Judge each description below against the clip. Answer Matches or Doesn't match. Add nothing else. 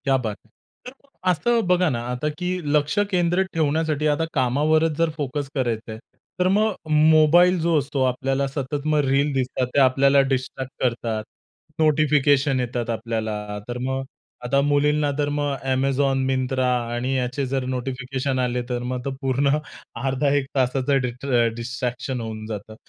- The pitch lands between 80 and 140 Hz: Matches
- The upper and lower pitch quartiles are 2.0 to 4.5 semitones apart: Matches